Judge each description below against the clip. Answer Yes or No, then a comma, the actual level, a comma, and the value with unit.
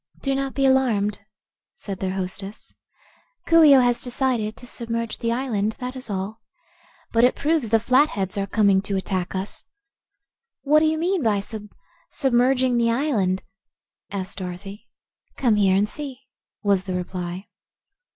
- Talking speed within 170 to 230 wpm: No, average, 160 wpm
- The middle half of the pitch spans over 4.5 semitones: Yes, average, 4.9 semitones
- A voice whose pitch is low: No, high, 225 Hz